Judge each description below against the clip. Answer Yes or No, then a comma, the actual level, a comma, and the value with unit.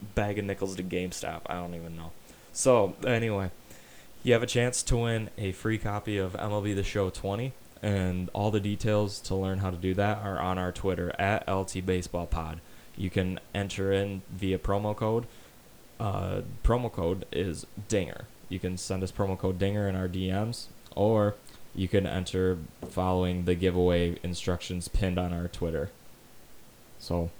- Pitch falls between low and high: No, very low, 95 Hz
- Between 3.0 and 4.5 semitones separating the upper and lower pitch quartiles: No, narrow, 2.4 semitones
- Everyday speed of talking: Yes, average, 170 wpm